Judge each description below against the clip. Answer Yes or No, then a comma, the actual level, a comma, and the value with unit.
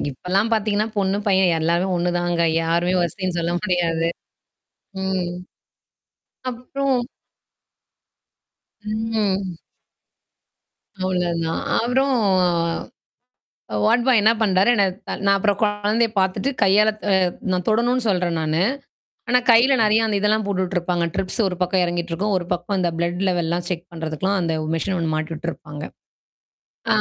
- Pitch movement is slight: No, average, 3.6 semitones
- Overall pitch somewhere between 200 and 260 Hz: No, medium, 185 Hz